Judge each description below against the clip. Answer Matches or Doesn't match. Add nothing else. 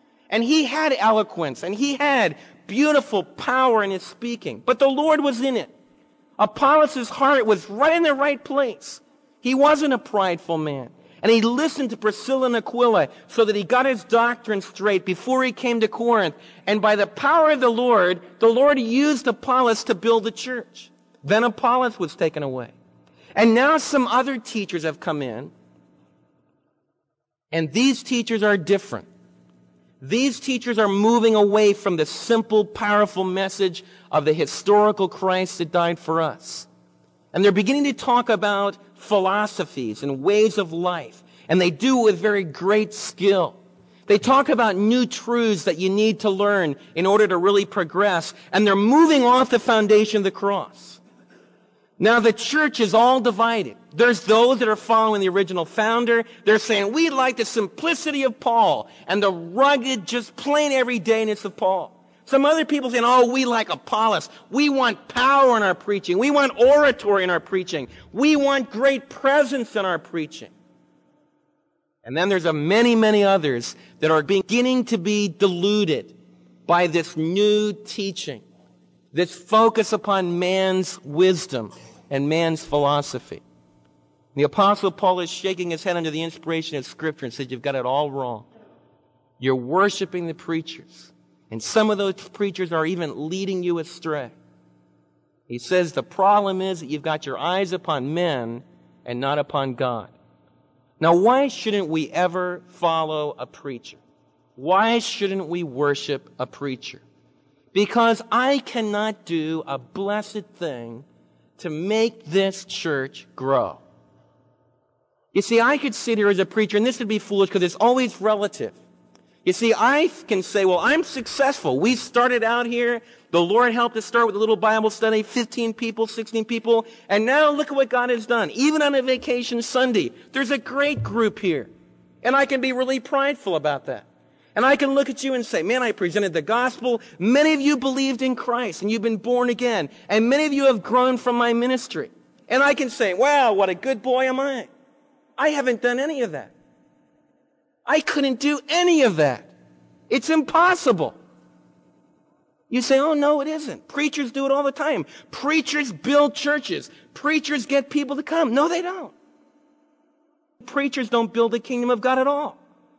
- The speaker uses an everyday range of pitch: Doesn't match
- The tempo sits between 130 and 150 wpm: Doesn't match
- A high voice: Matches